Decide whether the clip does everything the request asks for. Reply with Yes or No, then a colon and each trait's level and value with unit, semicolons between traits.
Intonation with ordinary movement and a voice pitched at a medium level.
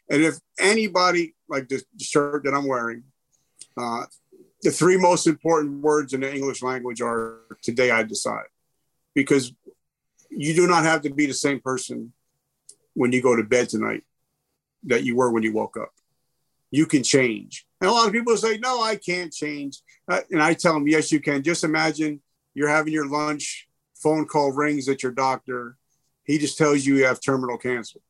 Yes: average, 3.3 semitones; medium, 145 Hz